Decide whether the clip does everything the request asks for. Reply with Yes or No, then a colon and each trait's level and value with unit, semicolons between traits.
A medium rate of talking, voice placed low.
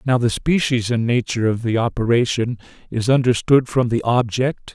Yes: average, 165 wpm; low, 120 Hz